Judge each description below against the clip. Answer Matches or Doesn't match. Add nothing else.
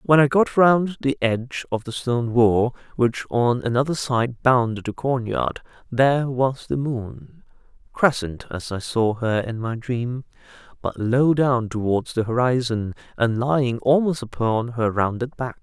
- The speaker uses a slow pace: Doesn't match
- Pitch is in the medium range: Doesn't match